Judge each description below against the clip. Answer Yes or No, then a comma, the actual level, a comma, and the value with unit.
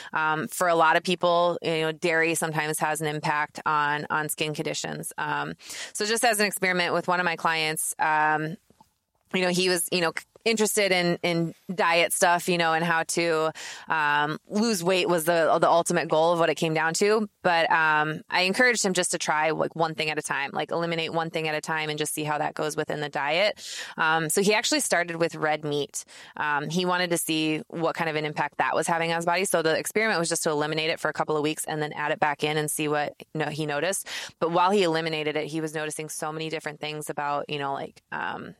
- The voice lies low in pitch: No, medium, 160 Hz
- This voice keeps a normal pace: No, fast, 245 wpm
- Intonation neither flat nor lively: No, narrow, 2.3 semitones